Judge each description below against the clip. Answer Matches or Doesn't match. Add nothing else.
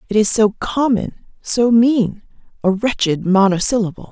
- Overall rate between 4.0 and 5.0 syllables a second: Matches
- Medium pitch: Doesn't match